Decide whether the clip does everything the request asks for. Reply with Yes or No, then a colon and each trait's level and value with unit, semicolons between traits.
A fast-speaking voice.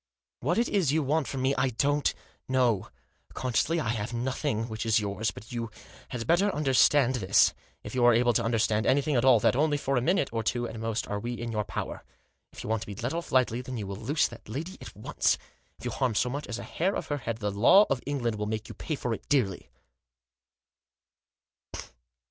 Yes: fast, 230 wpm